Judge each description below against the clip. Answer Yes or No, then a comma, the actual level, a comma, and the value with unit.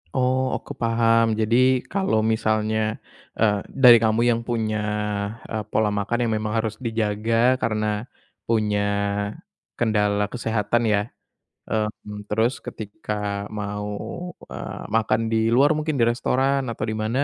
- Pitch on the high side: No, low, 110 Hz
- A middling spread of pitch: No, narrow, 1.8 semitones